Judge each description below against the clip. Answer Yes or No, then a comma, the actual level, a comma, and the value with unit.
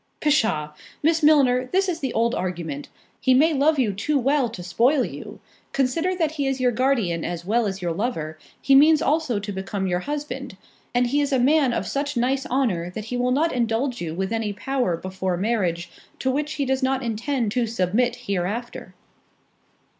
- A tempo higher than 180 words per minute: Yes, average, 190 wpm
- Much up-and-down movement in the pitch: Yes, wide, 6.0 semitones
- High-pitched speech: Yes, high, 245 Hz